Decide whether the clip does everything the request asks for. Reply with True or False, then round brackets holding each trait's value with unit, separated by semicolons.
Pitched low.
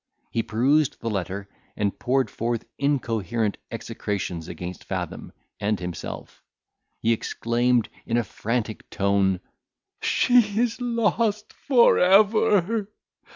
True (120 Hz)